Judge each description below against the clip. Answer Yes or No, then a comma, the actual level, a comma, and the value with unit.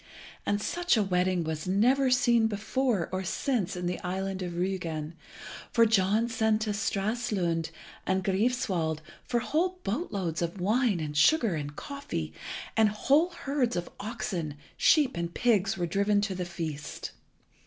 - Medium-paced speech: Yes, average, 155 wpm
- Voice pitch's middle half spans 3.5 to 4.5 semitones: No, average, 5.1 semitones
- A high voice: Yes, high, 200 Hz